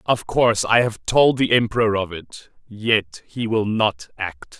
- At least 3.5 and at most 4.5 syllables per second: Yes, 4.1 syllables/s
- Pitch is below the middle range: Yes, low, 105 Hz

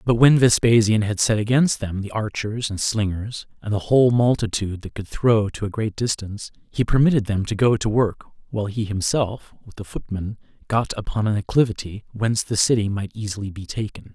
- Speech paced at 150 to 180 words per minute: No, average, 195 wpm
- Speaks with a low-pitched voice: Yes, low, 110 Hz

